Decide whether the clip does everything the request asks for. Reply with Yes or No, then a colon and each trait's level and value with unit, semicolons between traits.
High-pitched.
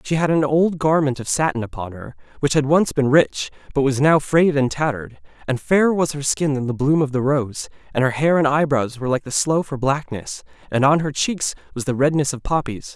No: medium, 140 Hz